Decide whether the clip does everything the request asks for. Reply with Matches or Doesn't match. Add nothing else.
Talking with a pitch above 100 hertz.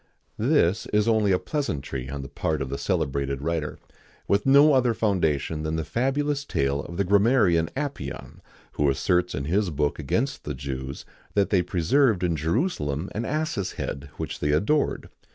Doesn't match